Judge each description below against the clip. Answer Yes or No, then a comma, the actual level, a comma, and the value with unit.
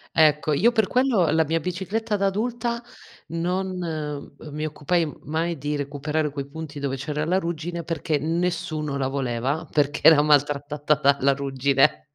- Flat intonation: No, average, 3.3 semitones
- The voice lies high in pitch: No, medium, 155 Hz